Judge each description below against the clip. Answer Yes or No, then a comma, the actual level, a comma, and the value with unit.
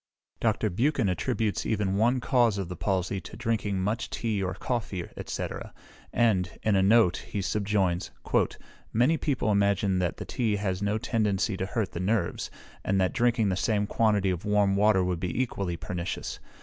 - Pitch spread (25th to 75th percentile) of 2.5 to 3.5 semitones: Yes, average, 3.1 semitones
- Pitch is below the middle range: Yes, low, 100 Hz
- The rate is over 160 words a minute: Yes, average, 170 wpm